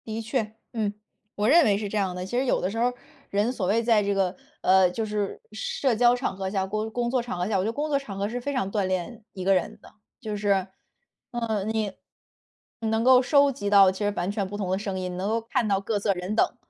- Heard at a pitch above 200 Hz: Yes, high, 210 Hz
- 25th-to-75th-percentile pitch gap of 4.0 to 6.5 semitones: No, average, 3.1 semitones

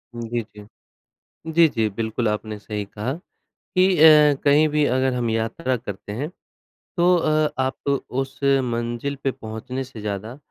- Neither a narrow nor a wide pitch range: Yes, average, 4.4 semitones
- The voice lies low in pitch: Yes, low, 125 Hz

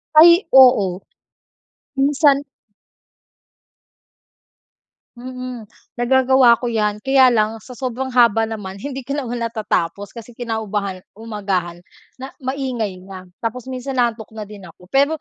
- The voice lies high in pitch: Yes, high, 235 Hz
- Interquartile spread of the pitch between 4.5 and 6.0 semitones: No, average, 3.9 semitones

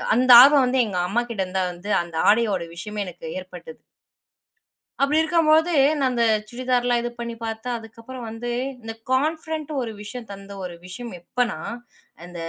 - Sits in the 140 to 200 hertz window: No, high, 235 Hz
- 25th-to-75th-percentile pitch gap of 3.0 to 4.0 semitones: No, average, 4.4 semitones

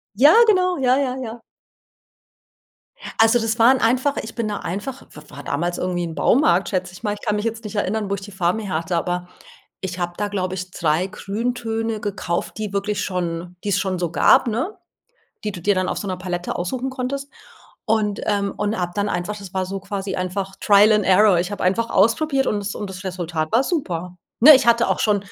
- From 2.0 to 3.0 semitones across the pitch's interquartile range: No, average, 3.8 semitones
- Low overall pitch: No, high, 205 Hz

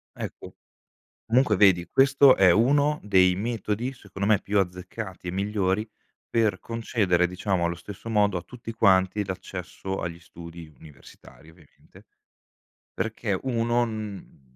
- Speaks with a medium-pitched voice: No, low, 100 Hz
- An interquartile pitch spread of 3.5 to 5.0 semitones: Yes, average, 4.0 semitones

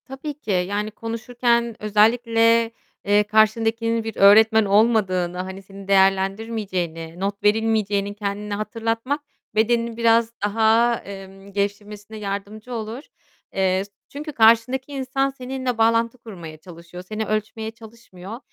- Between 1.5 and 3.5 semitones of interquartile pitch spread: Yes, narrow, 2.5 semitones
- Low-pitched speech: No, high, 220 Hz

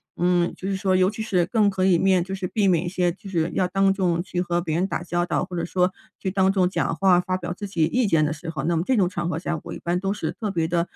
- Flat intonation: Yes, narrow, 1.9 semitones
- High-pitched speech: No, medium, 180 Hz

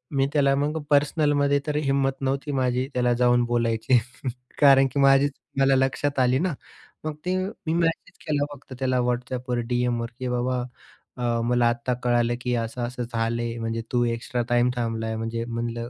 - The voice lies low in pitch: Yes, low, 125 Hz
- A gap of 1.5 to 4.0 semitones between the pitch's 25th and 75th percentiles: Yes, narrow, 2.5 semitones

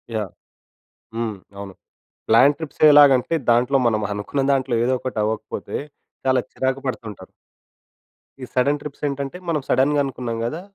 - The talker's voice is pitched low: Yes, low, 130 Hz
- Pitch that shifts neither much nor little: Yes, average, 3.6 semitones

